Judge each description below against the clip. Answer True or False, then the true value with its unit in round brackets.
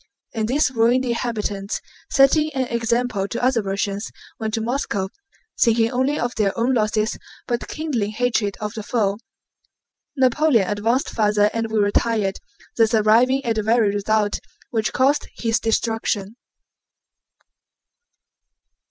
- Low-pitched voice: False (225 Hz)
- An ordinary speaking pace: False (130 wpm)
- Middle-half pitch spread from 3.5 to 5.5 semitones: False (2.8 semitones)